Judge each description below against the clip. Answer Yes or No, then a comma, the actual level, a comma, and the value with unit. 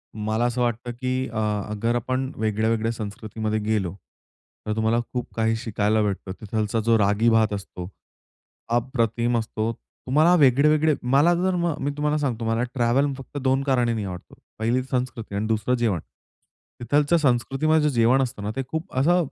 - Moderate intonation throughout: Yes, average, 3.5 semitones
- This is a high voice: No, low, 120 Hz